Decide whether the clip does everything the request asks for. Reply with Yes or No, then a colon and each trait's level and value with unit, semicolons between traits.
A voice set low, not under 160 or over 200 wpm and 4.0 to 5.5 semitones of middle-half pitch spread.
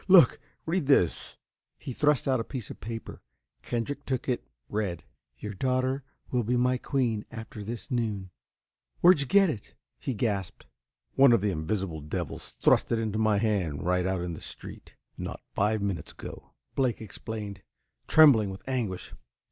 Yes: low, 110 Hz; average, 165 wpm; average, 4.5 semitones